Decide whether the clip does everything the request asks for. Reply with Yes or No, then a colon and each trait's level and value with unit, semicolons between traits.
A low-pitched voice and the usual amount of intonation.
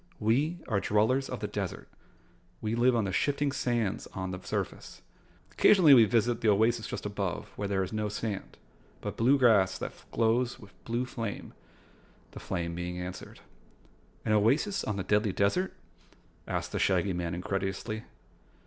Yes: low, 110 Hz; average, 3.6 semitones